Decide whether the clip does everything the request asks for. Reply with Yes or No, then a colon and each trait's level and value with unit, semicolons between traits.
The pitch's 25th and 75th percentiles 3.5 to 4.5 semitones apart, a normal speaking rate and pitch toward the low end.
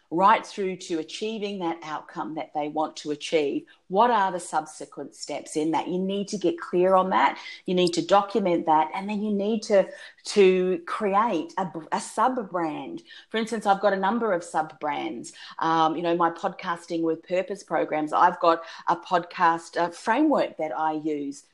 No: average, 3.8 semitones; average, 185 wpm; medium, 180 Hz